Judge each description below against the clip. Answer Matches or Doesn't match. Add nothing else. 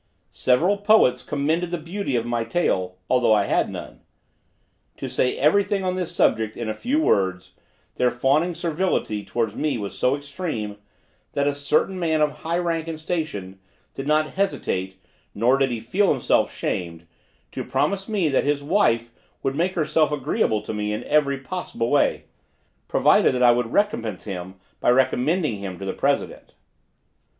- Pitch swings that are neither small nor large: Doesn't match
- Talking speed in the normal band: Matches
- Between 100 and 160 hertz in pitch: Matches